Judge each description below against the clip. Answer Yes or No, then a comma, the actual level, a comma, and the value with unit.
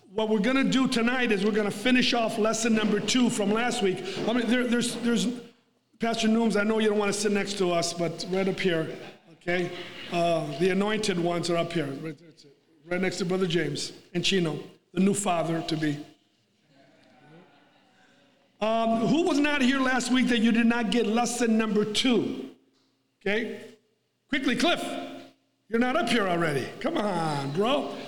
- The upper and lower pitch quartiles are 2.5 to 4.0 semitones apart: No, average, 4.8 semitones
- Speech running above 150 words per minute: Yes, average, 180 wpm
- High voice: Yes, high, 210 Hz